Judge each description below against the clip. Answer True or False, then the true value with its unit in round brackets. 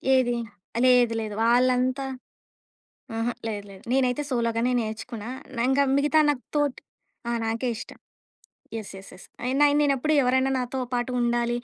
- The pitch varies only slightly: True (2.2 semitones)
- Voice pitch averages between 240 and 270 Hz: True (245 Hz)